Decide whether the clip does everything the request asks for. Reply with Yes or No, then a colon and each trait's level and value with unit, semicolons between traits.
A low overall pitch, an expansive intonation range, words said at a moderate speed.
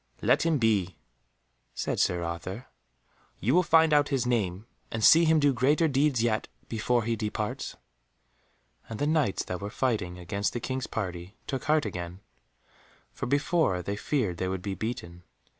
Yes: low, 115 Hz; wide, 7.2 semitones; average, 165 wpm